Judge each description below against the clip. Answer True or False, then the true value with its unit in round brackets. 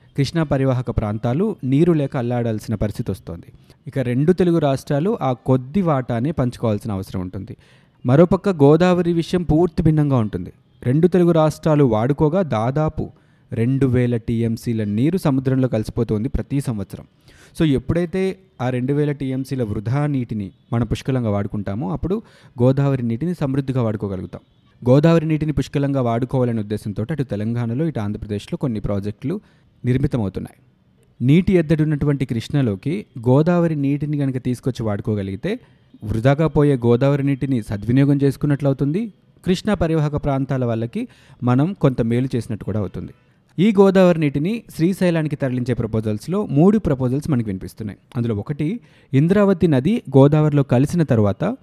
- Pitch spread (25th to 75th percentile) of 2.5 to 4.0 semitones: False (4.9 semitones)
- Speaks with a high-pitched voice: False (135 Hz)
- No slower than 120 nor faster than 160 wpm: True (125 wpm)